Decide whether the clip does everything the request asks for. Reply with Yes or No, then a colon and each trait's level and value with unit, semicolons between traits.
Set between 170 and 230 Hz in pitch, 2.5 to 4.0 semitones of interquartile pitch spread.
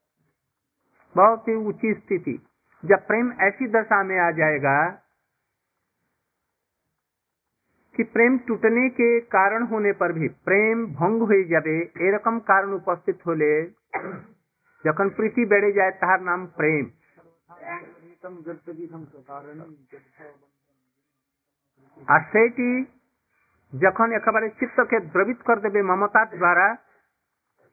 No: high, 190 Hz; wide, 5.5 semitones